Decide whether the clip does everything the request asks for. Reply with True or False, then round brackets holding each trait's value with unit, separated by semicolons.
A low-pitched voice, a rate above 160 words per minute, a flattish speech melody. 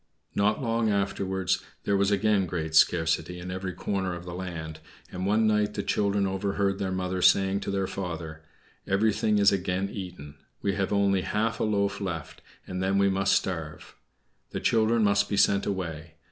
True (95 Hz; 175 wpm; 1.9 semitones)